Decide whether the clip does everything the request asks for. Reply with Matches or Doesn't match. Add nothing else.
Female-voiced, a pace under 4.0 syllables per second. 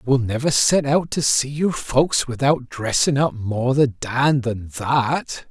Doesn't match